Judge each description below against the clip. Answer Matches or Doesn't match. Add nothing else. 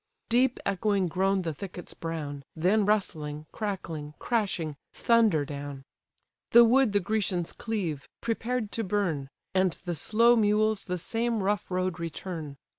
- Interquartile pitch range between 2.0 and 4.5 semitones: Doesn't match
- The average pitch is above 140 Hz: Matches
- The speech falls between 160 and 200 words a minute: Doesn't match